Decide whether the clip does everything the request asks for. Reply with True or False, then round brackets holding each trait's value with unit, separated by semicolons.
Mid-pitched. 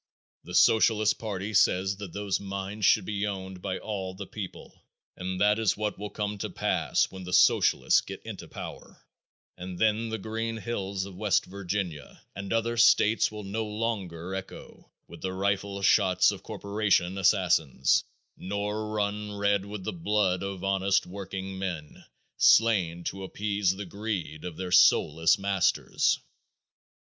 False (100 Hz)